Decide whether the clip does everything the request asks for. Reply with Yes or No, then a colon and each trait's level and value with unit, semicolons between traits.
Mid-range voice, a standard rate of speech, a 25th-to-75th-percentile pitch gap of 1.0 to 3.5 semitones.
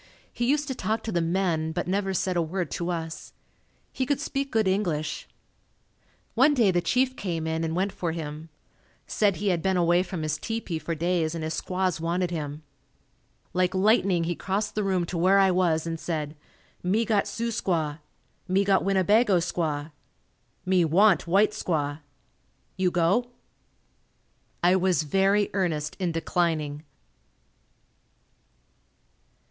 Yes: medium, 180 Hz; average, 155 wpm; average, 3.2 semitones